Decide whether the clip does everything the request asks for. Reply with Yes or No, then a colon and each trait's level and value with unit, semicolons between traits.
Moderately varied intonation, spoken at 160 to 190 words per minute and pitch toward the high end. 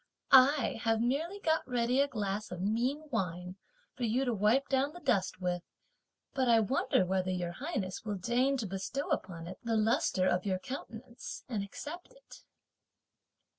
No: wide, 6.0 semitones; average, 170 wpm; high, 230 Hz